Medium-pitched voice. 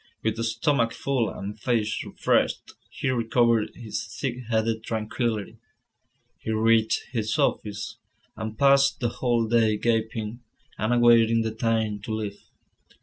No: low, 115 Hz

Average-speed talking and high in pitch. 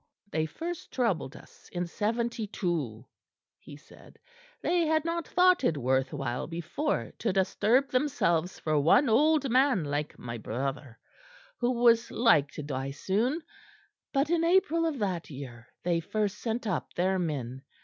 Yes: average, 150 wpm; high, 195 Hz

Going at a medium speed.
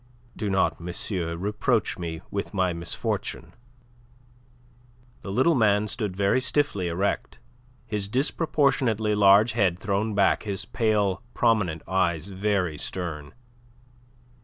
No: slow, 110 wpm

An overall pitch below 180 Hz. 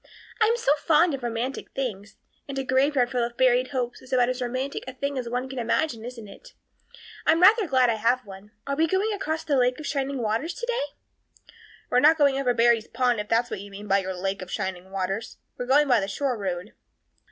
No: very high, 250 Hz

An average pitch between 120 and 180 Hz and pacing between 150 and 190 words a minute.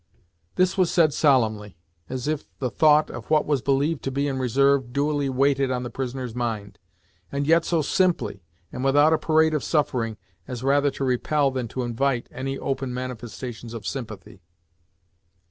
Yes: low, 135 Hz; average, 170 wpm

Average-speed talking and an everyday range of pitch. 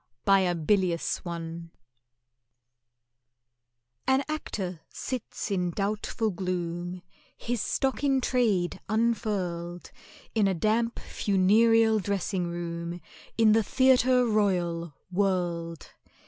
No: slow, 95 wpm; average, 4.5 semitones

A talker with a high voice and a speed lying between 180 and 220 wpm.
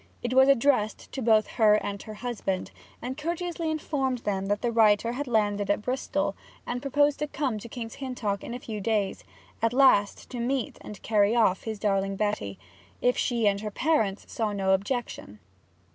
Yes: high, 225 Hz; average, 190 wpm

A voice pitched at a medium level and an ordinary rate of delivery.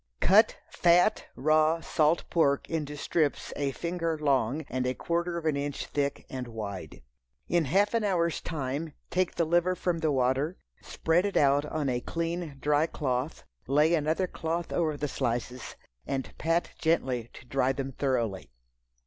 Yes: medium, 150 Hz; average, 160 wpm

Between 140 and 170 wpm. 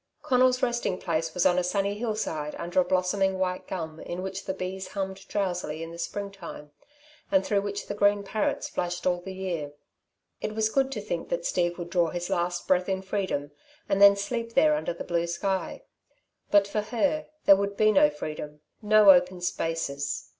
No: average, 195 wpm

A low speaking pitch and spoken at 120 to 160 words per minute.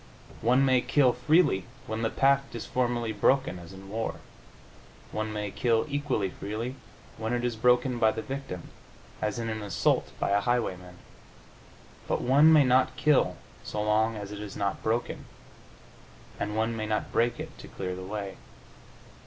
No: low, 115 Hz; average, 170 wpm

